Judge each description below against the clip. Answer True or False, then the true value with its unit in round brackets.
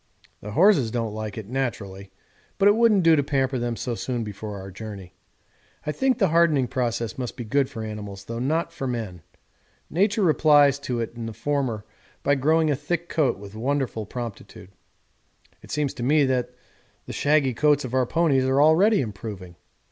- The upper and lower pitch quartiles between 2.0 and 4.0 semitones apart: False (5.3 semitones)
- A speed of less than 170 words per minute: False (185 wpm)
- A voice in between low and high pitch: False (130 Hz)